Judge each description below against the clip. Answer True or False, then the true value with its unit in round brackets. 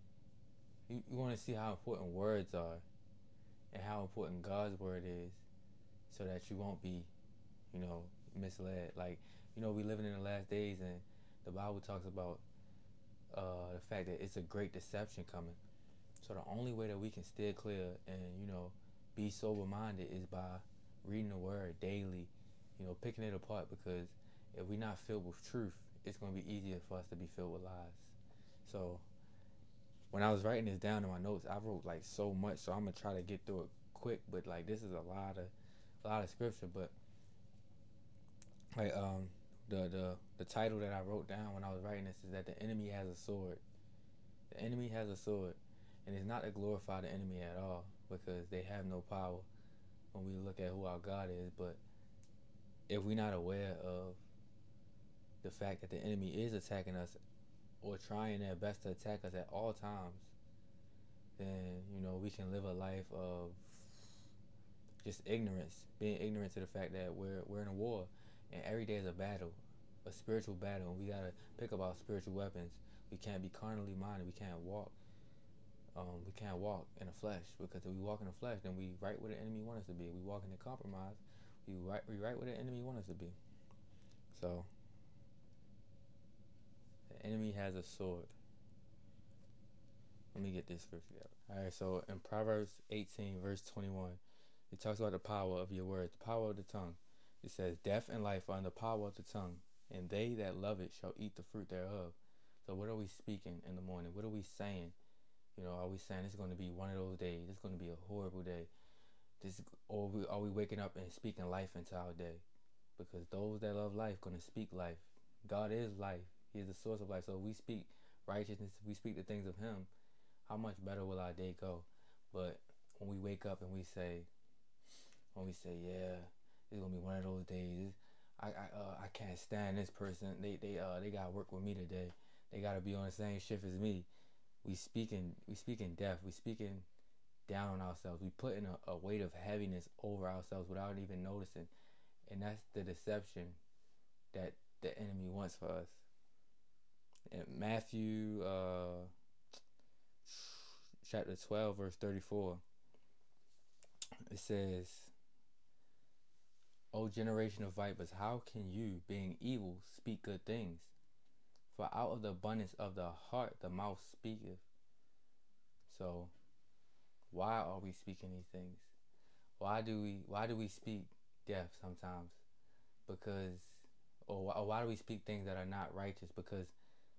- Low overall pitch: True (100 Hz)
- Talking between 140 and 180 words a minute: False (190 wpm)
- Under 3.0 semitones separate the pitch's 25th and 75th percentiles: True (2.5 semitones)